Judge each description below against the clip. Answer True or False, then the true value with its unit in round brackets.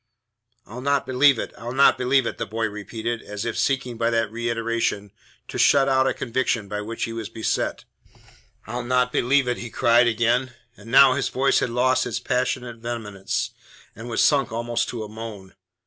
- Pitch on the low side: True (120 Hz)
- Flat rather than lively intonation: True (2.0 semitones)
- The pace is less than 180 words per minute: False (190 wpm)